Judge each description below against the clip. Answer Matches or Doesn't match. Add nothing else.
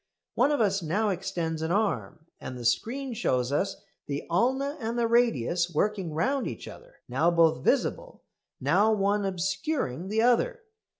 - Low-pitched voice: Doesn't match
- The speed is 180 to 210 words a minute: Doesn't match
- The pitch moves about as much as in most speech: Doesn't match